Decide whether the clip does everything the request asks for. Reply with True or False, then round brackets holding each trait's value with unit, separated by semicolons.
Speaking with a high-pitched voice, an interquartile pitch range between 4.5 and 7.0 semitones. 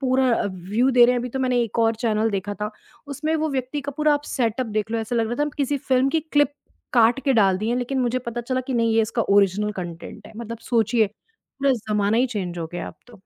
False (235 Hz; 3.7 semitones)